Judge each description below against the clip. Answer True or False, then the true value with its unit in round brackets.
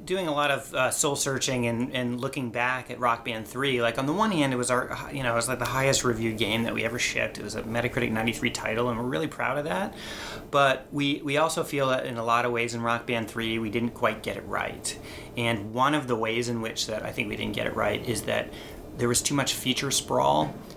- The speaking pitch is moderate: False (125 Hz)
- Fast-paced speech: True (265 wpm)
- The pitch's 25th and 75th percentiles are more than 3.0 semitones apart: False (2.7 semitones)